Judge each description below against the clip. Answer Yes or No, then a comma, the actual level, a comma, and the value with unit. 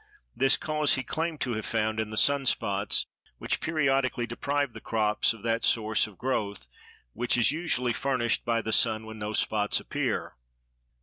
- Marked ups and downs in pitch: No, average, 3.7 semitones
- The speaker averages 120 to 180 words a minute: Yes, average, 175 wpm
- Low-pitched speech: Yes, low, 115 Hz